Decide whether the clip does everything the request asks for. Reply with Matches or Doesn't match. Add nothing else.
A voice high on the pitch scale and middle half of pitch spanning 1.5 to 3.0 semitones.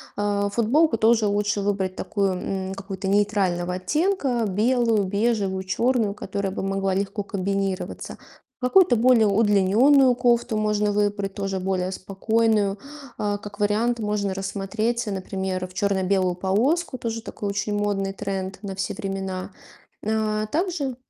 Matches